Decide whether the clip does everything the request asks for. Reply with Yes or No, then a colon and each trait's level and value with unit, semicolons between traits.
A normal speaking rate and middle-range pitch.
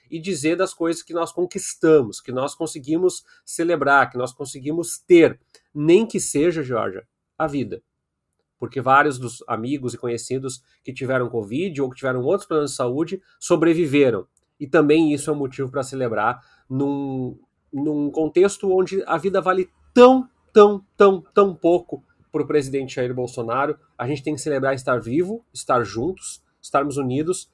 Yes: average, 160 wpm; medium, 150 Hz